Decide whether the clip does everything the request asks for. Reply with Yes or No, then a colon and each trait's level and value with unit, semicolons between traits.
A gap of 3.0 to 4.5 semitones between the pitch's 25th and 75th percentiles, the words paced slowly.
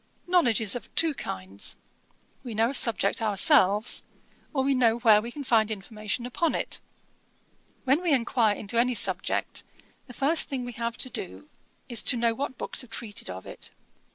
No: average, 3.5 semitones; average, 180 wpm